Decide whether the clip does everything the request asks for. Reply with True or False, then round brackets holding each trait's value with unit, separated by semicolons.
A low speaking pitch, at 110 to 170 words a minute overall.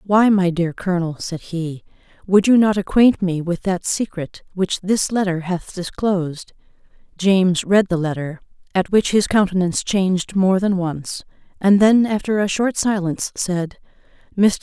False (190 Hz; 160 wpm)